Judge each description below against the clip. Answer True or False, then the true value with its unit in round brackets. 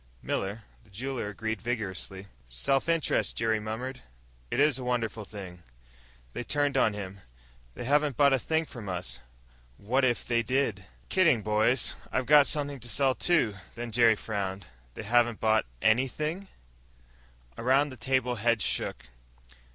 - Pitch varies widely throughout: False (4.2 semitones)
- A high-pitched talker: False (120 Hz)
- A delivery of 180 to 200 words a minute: False (150 wpm)